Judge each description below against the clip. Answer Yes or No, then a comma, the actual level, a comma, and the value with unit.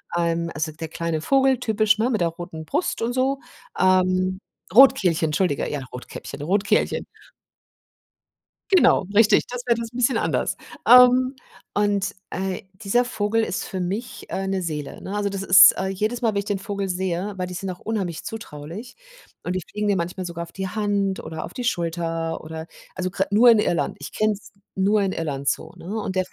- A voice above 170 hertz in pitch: Yes, high, 190 Hz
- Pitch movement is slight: No, average, 4.1 semitones